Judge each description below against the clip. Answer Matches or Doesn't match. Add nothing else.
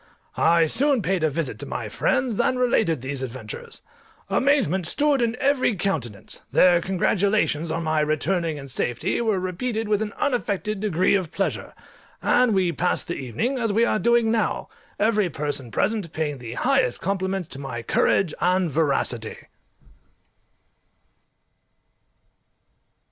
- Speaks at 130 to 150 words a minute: Matches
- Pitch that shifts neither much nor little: Doesn't match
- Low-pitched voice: Doesn't match